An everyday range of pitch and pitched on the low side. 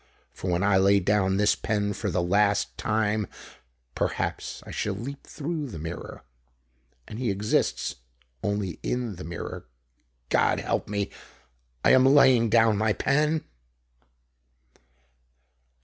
Yes: average, 3.4 semitones; low, 105 Hz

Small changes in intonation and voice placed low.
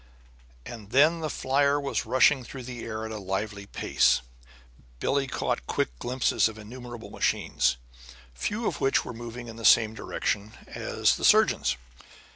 No: average, 3.8 semitones; low, 120 Hz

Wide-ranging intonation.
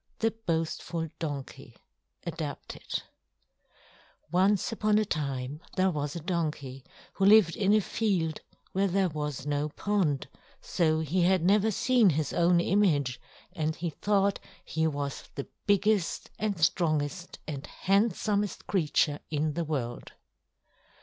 No: average, 4.9 semitones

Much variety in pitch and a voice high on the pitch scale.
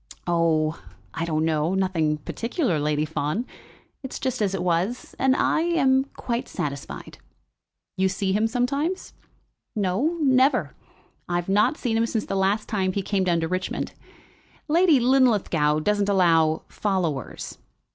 Yes: wide, 6.9 semitones; high, 195 Hz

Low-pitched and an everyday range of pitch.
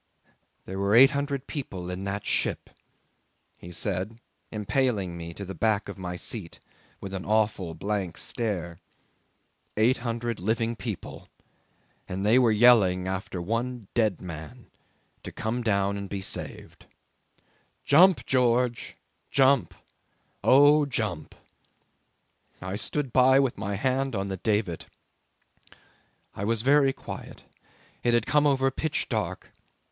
Yes: low, 110 Hz; average, 4.9 semitones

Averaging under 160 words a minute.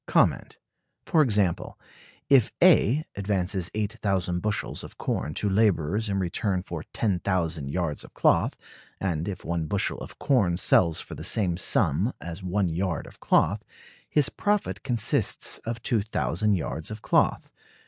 Yes: average, 140 wpm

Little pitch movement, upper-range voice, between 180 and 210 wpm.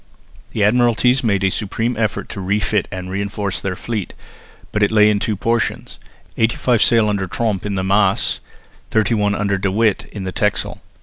No: narrow, 2.3 semitones; low, 105 Hz; average, 185 wpm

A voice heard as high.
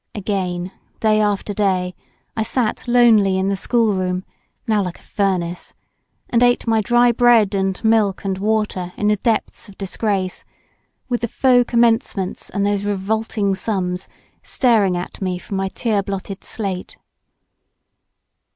Yes: high, 205 Hz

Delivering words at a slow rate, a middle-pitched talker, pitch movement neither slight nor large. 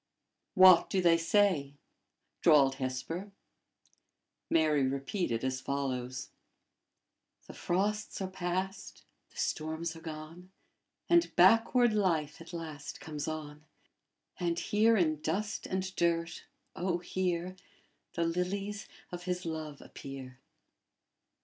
Yes: slow, 110 wpm; medium, 170 Hz; average, 3.8 semitones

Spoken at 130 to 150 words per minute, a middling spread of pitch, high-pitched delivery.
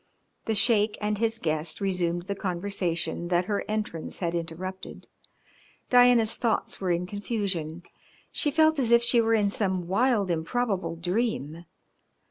Yes: average, 140 wpm; average, 4.5 semitones; high, 200 Hz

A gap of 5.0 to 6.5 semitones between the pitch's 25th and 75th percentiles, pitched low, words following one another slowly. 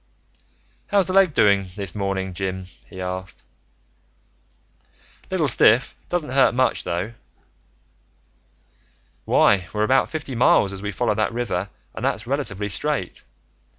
Yes: wide, 5.5 semitones; low, 105 Hz; slow, 120 wpm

